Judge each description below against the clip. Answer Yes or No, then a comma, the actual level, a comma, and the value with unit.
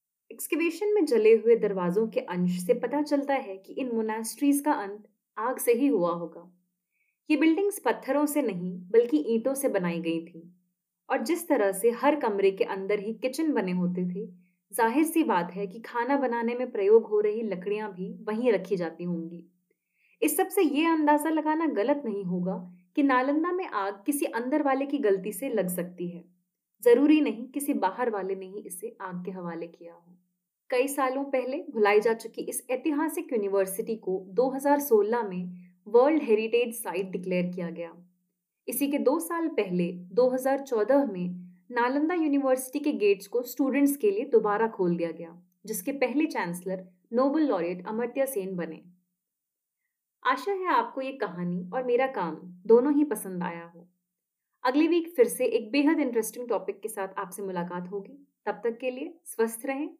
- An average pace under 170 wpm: No, average, 175 wpm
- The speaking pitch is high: Yes, high, 230 Hz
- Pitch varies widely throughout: Yes, wide, 7.6 semitones